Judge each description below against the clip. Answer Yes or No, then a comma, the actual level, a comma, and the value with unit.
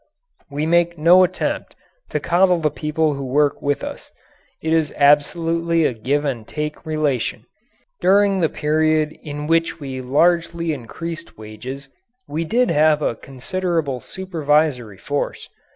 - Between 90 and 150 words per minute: Yes, slow, 135 wpm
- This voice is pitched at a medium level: Yes, medium, 155 Hz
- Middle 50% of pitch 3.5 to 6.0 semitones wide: No, average, 2.9 semitones